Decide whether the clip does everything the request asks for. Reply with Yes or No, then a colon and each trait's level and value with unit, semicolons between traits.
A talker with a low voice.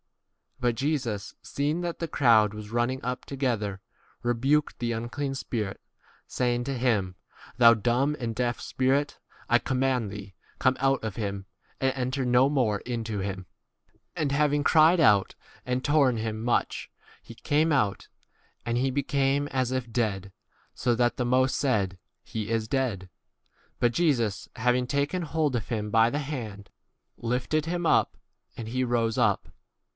Yes: low, 125 Hz